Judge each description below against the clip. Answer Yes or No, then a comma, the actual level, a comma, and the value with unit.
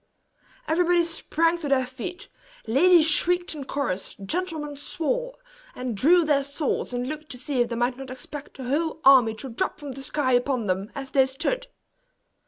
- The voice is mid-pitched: No, very high, 280 Hz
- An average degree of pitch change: Yes, average, 4.4 semitones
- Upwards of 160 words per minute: Yes, average, 180 wpm